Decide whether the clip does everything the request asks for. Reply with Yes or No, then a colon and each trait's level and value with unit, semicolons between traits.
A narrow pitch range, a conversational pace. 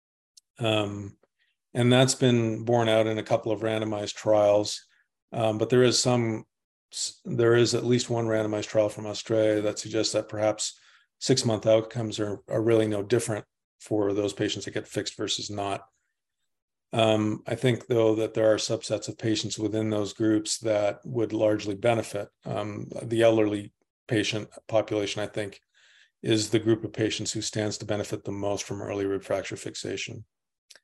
Yes: narrow, 1.4 semitones; average, 165 wpm